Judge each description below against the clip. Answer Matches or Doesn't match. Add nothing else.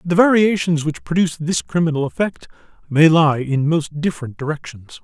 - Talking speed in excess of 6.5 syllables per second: Doesn't match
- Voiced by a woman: Doesn't match